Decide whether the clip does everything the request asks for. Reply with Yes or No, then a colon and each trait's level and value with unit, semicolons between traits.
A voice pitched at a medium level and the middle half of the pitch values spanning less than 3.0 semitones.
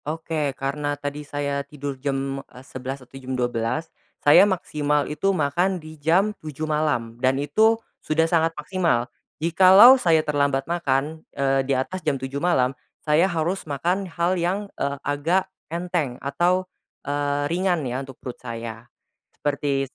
No: medium, 145 Hz; average, 3.8 semitones